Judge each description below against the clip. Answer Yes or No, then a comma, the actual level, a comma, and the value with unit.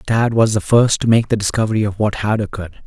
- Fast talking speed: Yes, fast, 250 wpm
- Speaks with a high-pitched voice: No, low, 110 Hz